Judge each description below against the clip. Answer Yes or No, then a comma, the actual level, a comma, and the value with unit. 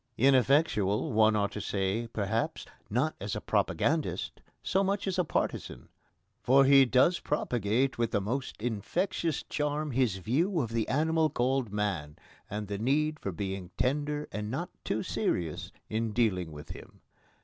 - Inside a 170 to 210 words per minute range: No, average, 155 wpm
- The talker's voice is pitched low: Yes, low, 120 Hz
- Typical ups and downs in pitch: No, wide, 6.0 semitones